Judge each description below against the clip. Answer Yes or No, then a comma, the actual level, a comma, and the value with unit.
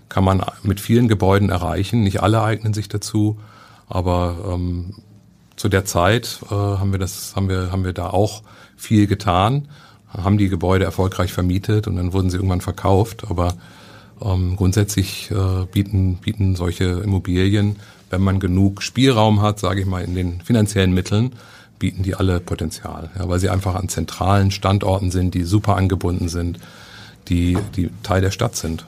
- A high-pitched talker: No, very low, 95 Hz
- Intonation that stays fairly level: Yes, narrow, 2.3 semitones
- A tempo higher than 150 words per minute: Yes, average, 170 wpm